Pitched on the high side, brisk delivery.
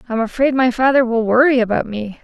Yes: high, 245 Hz; fast, 215 wpm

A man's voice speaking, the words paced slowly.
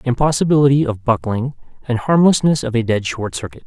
No: male; average, 165 wpm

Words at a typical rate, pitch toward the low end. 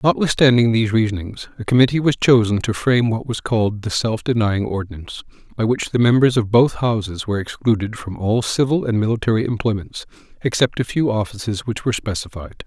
Yes: average, 180 wpm; low, 110 Hz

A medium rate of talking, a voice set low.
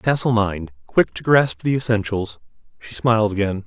Yes: average, 145 wpm; low, 110 Hz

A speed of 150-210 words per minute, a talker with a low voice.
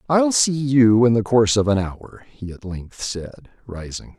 Yes: average, 200 wpm; low, 115 Hz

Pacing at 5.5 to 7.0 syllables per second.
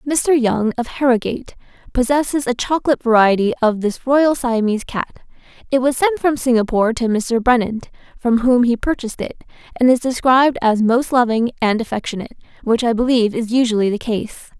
Yes: 5.8 syllables/s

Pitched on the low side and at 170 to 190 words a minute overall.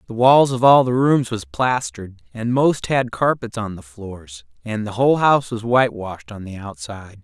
No: low, 115 Hz; average, 200 wpm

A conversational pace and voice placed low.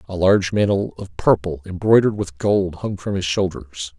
Yes: average, 180 wpm; very low, 95 Hz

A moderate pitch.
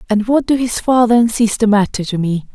No: high, 220 Hz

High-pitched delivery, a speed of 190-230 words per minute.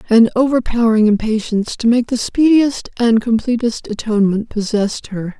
No: high, 230 Hz; slow, 135 wpm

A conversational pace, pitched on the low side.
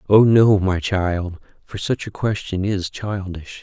Yes: average, 165 wpm; very low, 95 Hz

